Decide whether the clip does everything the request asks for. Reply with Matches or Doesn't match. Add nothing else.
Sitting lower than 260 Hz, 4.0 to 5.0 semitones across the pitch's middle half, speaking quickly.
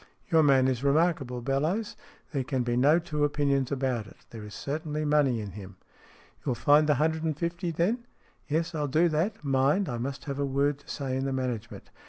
Doesn't match